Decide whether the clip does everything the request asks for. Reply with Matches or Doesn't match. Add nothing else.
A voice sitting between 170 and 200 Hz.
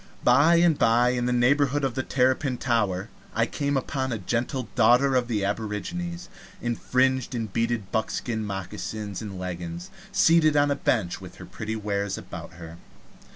Doesn't match